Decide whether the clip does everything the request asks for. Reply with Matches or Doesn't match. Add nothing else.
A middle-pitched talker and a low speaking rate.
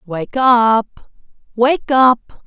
Doesn't match